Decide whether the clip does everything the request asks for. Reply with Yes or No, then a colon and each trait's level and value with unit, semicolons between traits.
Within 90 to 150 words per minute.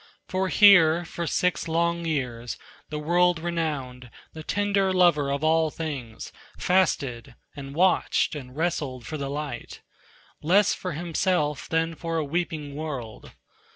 Yes: average, 140 wpm